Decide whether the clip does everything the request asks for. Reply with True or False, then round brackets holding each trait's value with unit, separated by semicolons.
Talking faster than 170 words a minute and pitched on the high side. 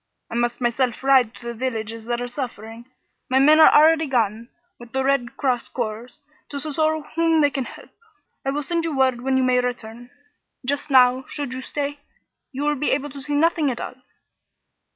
True (195 wpm; 260 Hz)